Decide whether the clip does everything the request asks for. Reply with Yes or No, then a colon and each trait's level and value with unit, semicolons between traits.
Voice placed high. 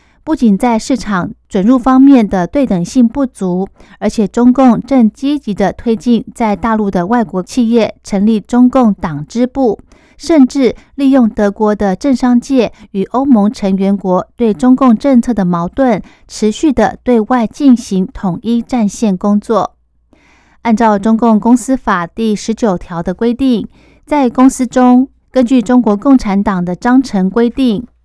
Yes: high, 230 Hz